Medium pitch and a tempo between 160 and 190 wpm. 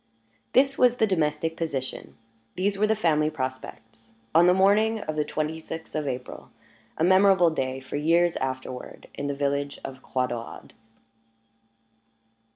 No: medium, 155 Hz; average, 150 wpm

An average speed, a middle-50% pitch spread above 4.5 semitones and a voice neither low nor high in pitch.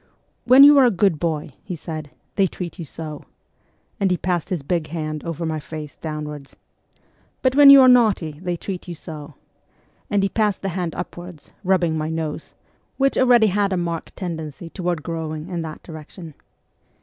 No: average, 190 wpm; average, 3.7 semitones; medium, 170 Hz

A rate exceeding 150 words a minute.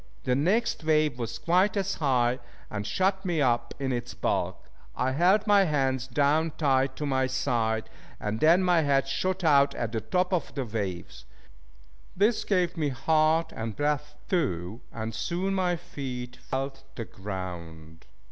Yes: average, 160 wpm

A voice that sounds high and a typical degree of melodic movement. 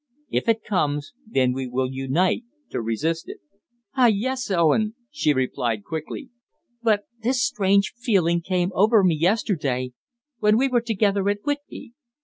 No: high, 195 Hz; wide, 7.2 semitones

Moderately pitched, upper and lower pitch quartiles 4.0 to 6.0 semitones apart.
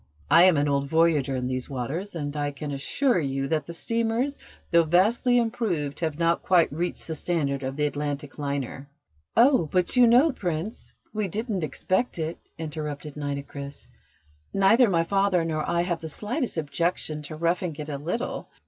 Yes: medium, 165 Hz; average, 5.1 semitones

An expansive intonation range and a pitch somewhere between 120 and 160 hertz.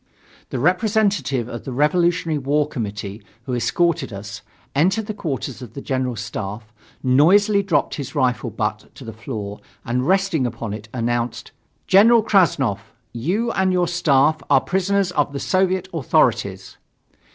Yes: wide, 7.5 semitones; medium, 140 Hz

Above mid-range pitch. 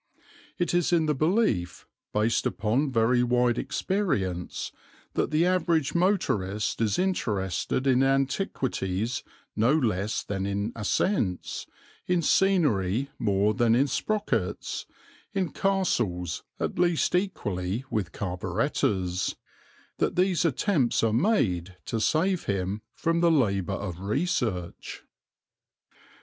No: low, 120 Hz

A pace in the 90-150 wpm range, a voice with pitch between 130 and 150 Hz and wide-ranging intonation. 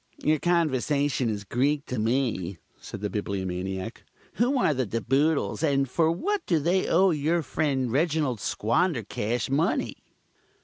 Yes: average, 140 wpm; medium, 140 Hz; wide, 6.0 semitones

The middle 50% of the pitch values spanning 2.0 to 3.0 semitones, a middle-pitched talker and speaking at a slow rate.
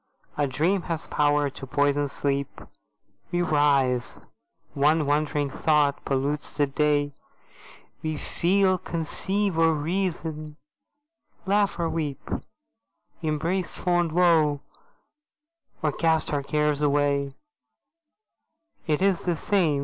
Yes: average, 2.7 semitones; medium, 150 Hz; slow, 105 wpm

